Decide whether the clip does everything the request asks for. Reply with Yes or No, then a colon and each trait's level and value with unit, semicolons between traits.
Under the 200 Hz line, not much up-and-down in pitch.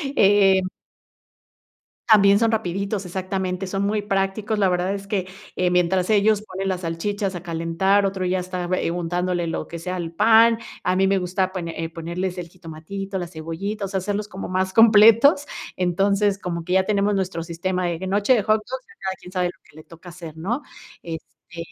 Yes: high, 190 Hz; narrow, 2.3 semitones